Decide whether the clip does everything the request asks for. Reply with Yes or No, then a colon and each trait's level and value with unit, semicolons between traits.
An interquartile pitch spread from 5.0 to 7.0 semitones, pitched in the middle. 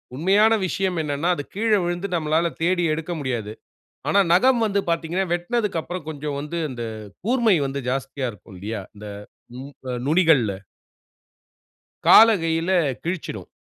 Yes: average, 5.3 semitones; medium, 170 Hz